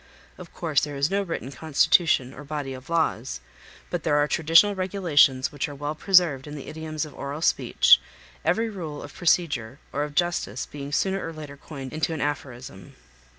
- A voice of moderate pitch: Yes, medium, 150 Hz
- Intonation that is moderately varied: Yes, average, 3.1 semitones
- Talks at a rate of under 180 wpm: No, average, 185 wpm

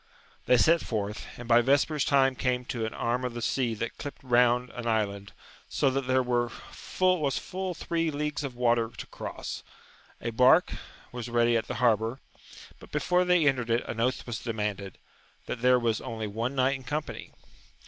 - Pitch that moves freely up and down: No, average, 2.9 semitones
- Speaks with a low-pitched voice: Yes, low, 125 Hz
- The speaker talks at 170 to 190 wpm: Yes, average, 180 wpm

